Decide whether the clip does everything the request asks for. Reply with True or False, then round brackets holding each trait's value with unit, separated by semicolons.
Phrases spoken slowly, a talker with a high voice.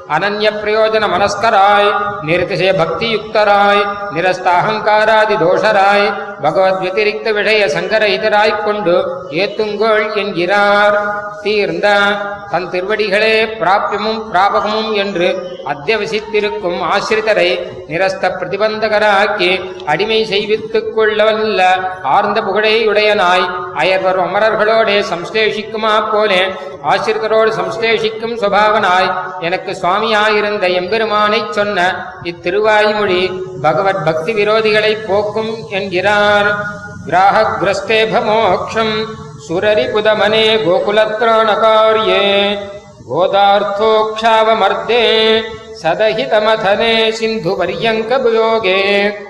True (65 wpm; 205 Hz)